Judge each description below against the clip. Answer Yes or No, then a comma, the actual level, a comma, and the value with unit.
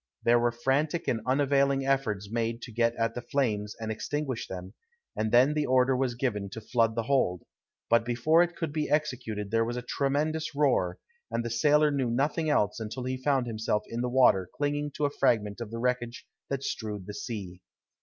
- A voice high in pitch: No, low, 120 Hz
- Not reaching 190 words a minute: No, average, 200 wpm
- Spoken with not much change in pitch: No, average, 3.7 semitones